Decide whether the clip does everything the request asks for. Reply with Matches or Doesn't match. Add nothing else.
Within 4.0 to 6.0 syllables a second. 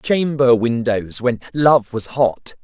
Doesn't match